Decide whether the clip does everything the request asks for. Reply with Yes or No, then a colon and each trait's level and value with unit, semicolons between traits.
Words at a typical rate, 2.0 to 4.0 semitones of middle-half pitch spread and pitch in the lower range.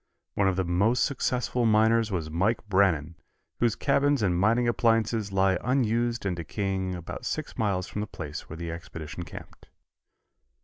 No: average, 160 wpm; average, 4.4 semitones; low, 100 Hz